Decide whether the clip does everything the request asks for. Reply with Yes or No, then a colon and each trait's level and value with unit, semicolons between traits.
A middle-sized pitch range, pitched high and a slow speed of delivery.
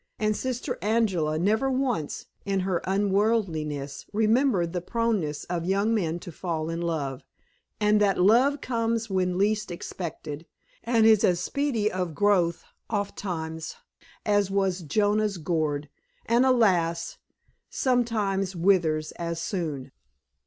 Yes: average, 4.5 semitones; high, 195 Hz; slow, 125 wpm